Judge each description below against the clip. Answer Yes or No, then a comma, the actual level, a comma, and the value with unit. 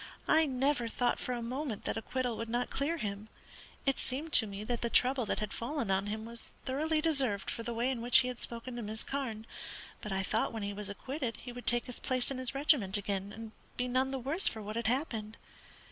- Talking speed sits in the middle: No, fast, 235 wpm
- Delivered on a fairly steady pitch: No, average, 3.5 semitones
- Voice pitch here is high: Yes, high, 240 Hz